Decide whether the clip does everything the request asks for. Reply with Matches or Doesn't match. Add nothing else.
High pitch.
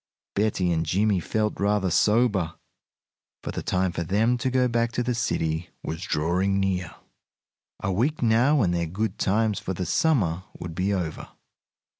Doesn't match